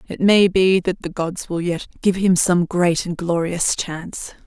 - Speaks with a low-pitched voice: No, medium, 180 Hz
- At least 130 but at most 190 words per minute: No, average, 200 wpm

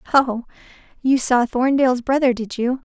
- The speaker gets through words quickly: No, average, 145 wpm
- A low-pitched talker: No, very high, 250 Hz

